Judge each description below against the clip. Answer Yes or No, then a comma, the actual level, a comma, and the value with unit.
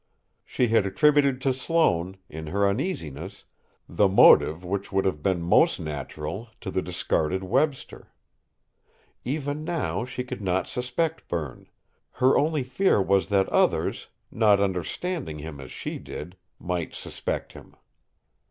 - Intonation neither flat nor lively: No, wide, 7.0 semitones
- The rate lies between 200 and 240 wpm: No, slow, 135 wpm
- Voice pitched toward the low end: Yes, low, 100 Hz